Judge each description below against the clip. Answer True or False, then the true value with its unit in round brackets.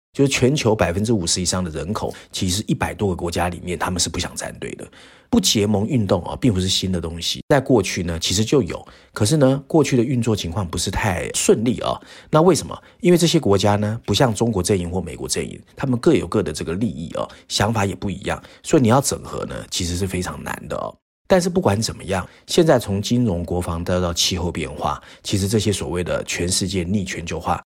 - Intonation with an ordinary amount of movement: True (4.7 semitones)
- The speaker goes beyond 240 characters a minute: True (340 characters per minute)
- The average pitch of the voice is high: False (100 Hz)